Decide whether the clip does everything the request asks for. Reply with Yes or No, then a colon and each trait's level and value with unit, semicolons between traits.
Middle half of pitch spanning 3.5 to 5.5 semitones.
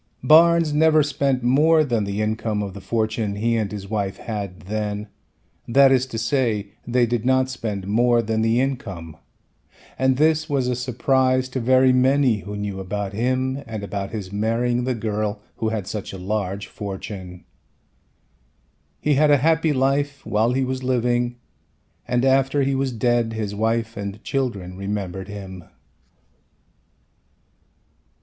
Yes: average, 4.1 semitones